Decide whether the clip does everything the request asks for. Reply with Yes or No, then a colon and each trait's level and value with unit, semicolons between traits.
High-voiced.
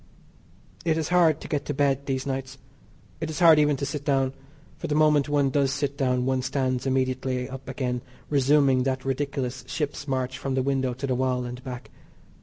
No: low, 135 Hz